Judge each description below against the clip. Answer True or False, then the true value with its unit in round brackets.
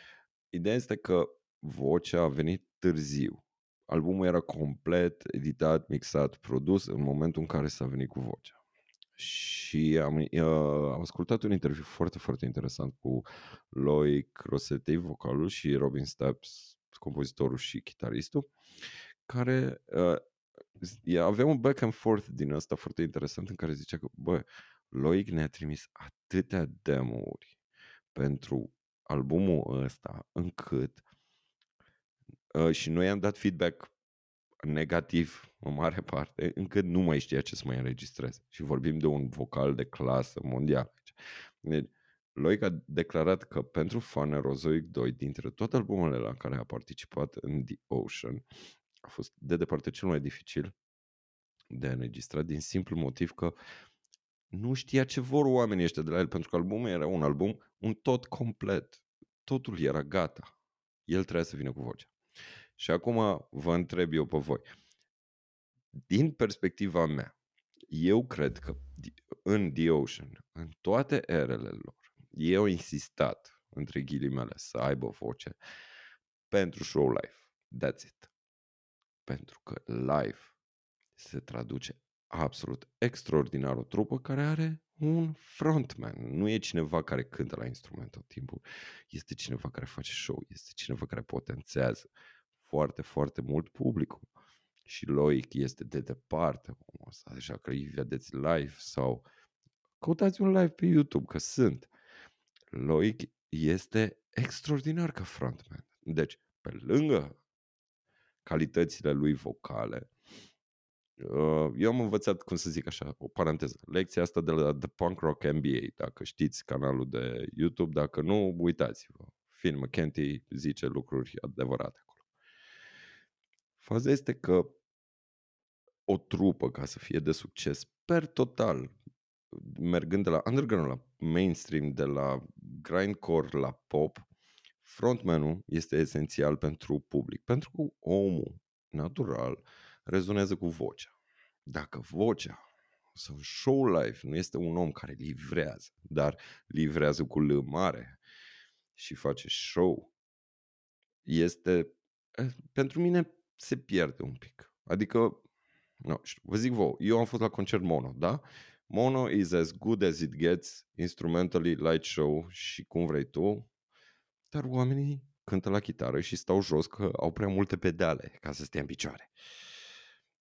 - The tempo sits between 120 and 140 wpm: True (135 wpm)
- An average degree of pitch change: False (6.1 semitones)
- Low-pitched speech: True (80 Hz)